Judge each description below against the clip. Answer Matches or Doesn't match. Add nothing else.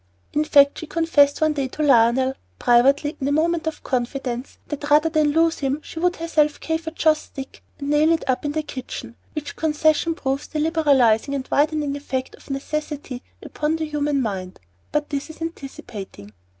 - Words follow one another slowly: Doesn't match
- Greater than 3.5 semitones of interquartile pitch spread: Doesn't match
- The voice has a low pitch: Doesn't match